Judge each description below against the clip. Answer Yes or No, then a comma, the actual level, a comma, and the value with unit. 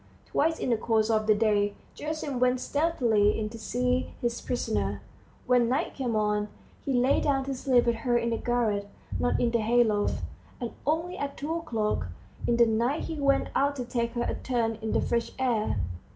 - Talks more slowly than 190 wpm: No, average, 200 wpm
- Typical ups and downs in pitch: Yes, average, 3.3 semitones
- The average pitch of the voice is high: Yes, high, 240 Hz